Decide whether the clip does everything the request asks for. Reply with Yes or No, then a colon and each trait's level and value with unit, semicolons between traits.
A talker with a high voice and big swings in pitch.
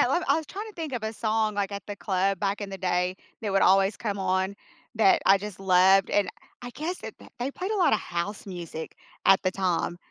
No: high, 200 Hz; average, 2.8 semitones